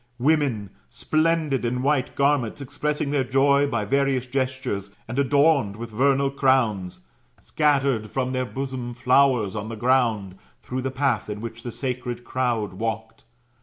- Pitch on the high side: No, low, 130 Hz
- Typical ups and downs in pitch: Yes, average, 3.5 semitones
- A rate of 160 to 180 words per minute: No, average, 150 wpm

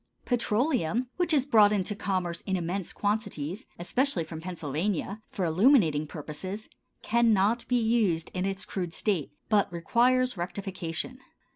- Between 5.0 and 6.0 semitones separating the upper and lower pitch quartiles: Yes, average, 5.3 semitones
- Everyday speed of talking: No, slow, 130 wpm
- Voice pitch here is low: No, high, 195 Hz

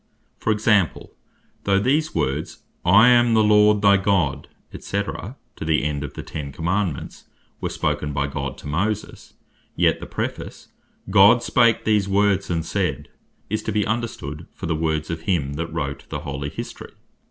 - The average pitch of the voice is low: Yes, very low, 95 Hz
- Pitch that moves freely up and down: Yes, wide, 5.8 semitones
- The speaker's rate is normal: Yes, average, 165 wpm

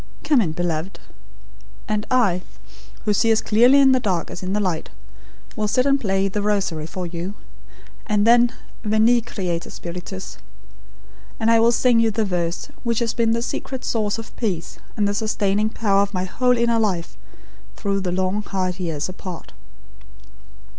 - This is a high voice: Yes, high, 205 Hz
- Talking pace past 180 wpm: No, average, 170 wpm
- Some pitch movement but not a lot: Yes, average, 3.8 semitones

